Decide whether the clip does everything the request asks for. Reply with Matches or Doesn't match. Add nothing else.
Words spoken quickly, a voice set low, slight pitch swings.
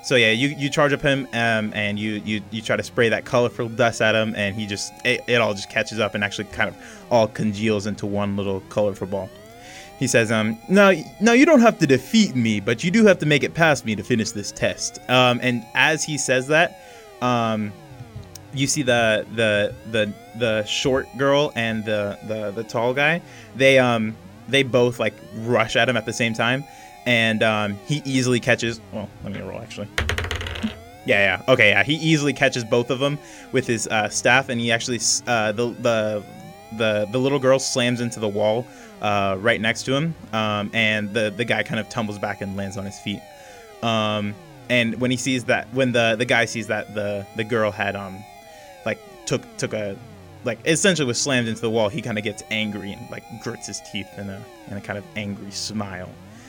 Doesn't match